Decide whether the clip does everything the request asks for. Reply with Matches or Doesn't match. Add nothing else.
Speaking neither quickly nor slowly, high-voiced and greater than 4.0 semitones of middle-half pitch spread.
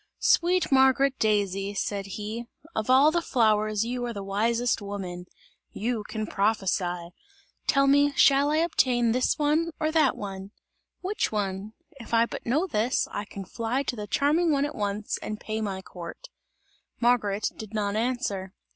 Matches